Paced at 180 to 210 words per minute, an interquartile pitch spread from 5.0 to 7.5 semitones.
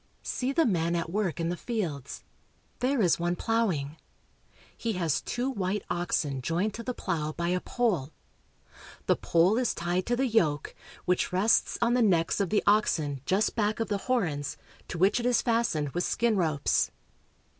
Yes: average, 185 wpm; wide, 5.4 semitones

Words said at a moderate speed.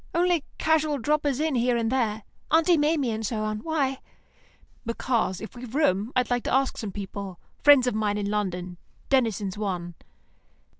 Yes: average, 165 wpm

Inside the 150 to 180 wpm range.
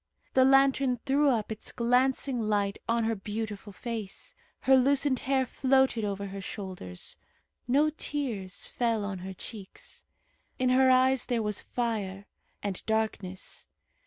No: slow, 135 wpm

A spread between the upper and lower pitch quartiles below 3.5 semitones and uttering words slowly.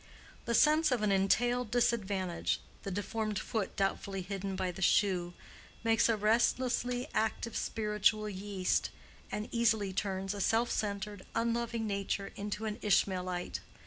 Yes: average, 2.9 semitones; slow, 130 wpm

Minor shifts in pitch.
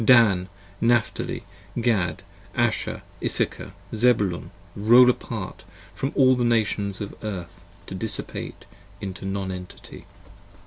No: average, 3.9 semitones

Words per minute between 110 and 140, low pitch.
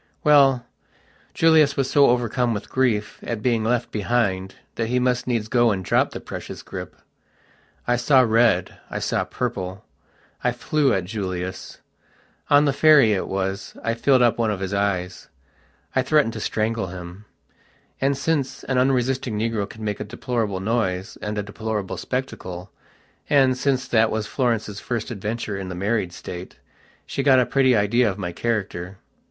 No: average, 165 wpm; low, 115 Hz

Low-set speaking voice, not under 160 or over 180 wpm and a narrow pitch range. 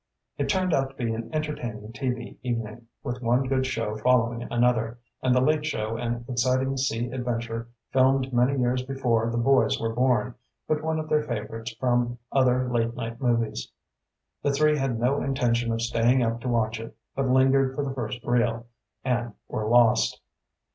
Yes: low, 120 Hz; average, 175 wpm; narrow, 2.3 semitones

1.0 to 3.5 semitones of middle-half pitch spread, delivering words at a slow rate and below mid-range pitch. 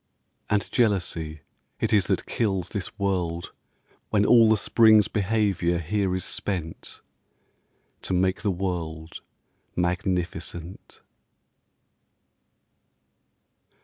Yes: average, 3.1 semitones; slow, 90 wpm; very low, 95 Hz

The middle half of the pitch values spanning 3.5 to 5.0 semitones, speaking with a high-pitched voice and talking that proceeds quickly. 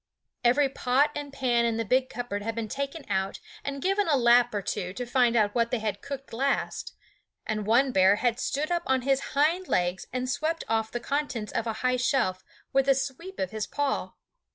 Yes: average, 3.8 semitones; very high, 250 Hz; fast, 210 wpm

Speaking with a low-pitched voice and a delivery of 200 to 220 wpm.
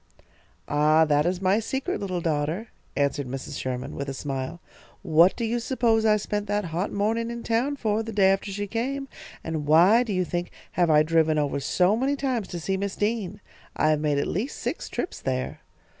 No: high, 190 Hz; fast, 205 wpm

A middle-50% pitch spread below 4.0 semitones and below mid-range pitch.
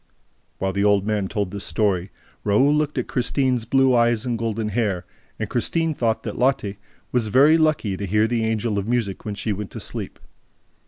Yes: average, 3.6 semitones; low, 110 Hz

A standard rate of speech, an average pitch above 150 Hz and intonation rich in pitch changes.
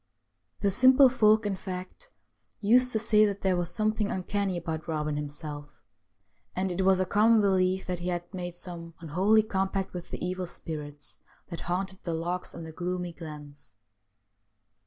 No: average, 170 wpm; medium, 185 Hz; average, 3.2 semitones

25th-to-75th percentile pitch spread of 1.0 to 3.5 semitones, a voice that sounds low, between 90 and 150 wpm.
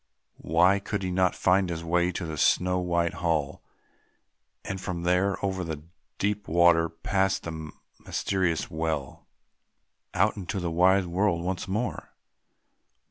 Yes: narrow, 2.4 semitones; very low, 90 Hz; slow, 135 wpm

